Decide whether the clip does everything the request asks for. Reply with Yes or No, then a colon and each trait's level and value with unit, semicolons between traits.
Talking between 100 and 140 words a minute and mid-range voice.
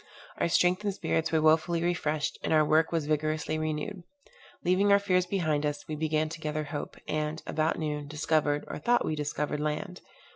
No: average, 190 wpm; medium, 155 Hz